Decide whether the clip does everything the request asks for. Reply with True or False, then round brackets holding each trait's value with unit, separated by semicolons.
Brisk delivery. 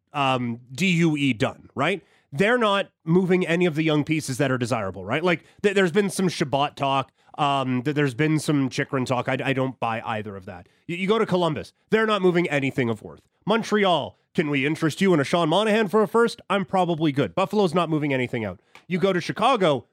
True (215 wpm)